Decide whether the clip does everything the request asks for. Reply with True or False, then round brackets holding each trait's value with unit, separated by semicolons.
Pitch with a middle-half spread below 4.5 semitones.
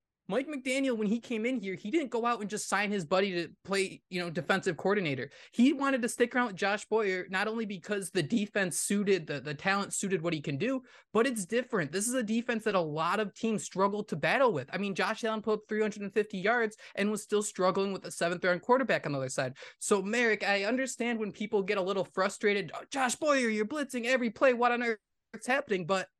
True (3.8 semitones)